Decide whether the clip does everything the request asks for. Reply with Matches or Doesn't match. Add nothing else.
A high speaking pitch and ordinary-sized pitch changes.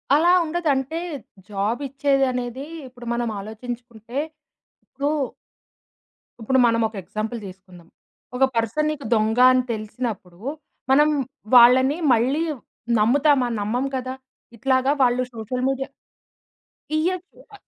Matches